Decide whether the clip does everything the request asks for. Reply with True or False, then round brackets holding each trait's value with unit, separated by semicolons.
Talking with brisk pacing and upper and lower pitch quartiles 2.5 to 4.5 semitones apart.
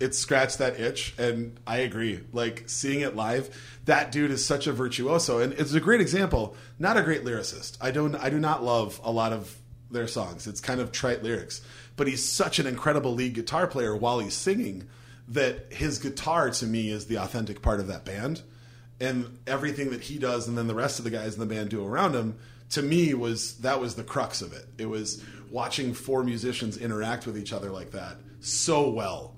True (215 wpm; 2.8 semitones)